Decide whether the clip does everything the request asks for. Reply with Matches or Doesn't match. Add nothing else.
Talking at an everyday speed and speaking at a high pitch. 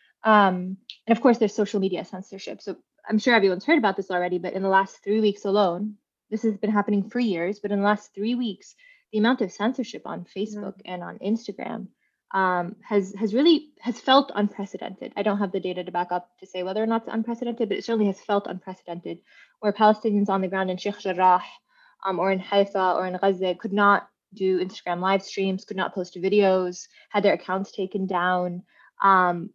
Doesn't match